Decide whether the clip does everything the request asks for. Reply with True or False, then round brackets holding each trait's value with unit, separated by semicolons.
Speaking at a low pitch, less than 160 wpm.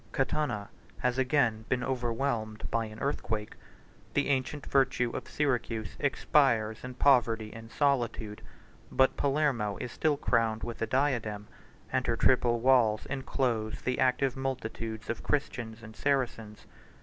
True (125 Hz; 140 wpm)